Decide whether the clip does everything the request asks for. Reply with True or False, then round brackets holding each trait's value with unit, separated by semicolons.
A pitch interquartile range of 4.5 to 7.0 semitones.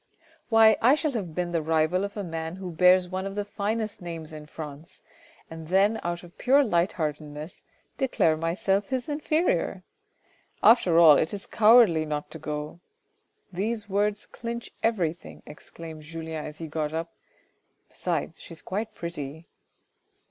True (4.8 semitones)